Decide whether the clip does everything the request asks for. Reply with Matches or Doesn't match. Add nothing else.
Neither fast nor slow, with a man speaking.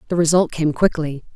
Doesn't match